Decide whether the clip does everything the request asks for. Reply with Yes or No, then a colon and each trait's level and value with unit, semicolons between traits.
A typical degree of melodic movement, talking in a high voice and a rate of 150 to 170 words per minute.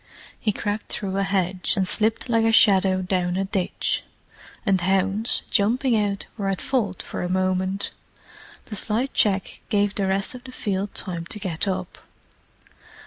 No: narrow, 2.2 semitones; high, 195 Hz; average, 165 wpm